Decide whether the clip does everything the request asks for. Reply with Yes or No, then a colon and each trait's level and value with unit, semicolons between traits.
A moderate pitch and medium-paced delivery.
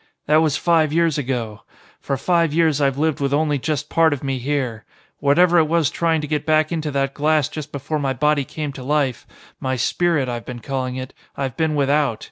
No: medium, 145 Hz; fast, 210 wpm